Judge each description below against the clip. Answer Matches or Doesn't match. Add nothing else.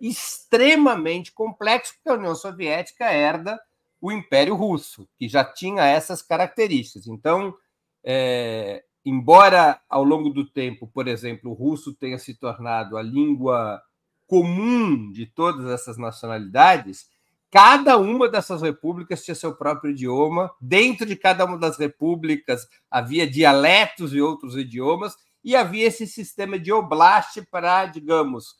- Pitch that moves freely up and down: Matches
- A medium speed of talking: Matches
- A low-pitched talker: Doesn't match